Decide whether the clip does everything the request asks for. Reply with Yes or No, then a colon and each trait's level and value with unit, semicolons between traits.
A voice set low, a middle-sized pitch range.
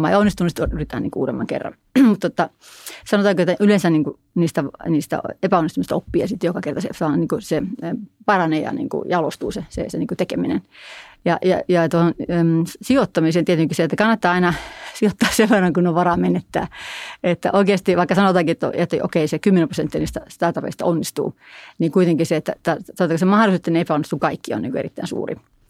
No: medium, 175 Hz; average, 3.0 semitones